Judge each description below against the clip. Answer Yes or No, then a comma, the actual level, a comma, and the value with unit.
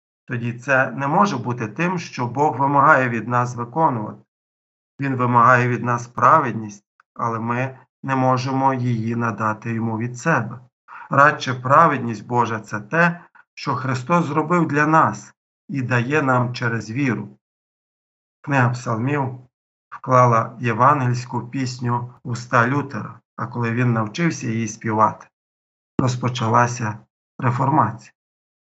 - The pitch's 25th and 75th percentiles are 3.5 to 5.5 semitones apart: No, average, 2.8 semitones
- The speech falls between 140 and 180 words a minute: No, average, 120 wpm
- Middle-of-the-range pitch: No, low, 125 Hz